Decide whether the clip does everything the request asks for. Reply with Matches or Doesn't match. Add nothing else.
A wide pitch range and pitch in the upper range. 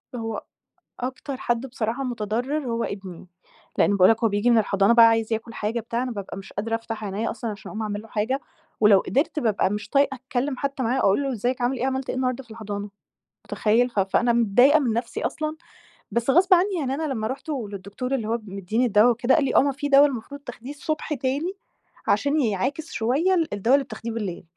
Doesn't match